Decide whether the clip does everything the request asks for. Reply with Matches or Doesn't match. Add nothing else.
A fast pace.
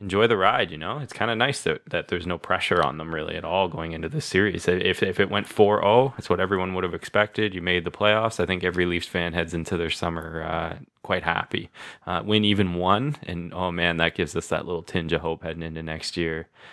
Matches